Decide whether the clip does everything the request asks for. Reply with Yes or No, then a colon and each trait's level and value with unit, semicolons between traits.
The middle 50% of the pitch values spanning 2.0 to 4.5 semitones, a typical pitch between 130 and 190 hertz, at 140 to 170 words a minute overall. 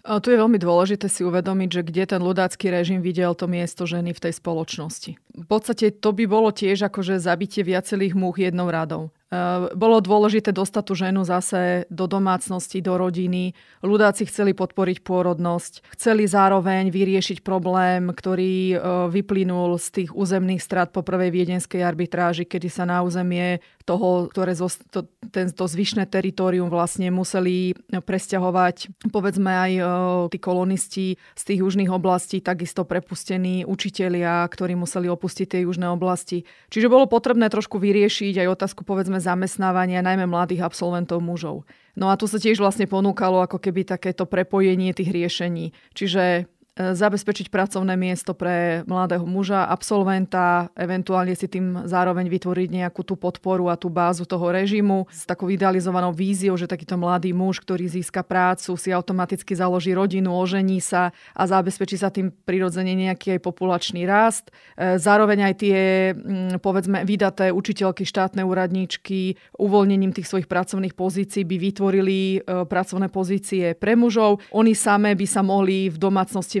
No: narrow, 1.4 semitones; medium, 185 Hz; average, 150 wpm